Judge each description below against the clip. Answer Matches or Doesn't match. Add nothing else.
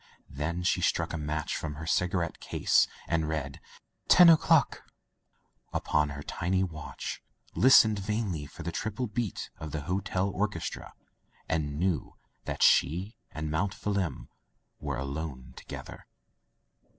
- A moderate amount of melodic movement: Matches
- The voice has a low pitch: Matches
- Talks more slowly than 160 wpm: Matches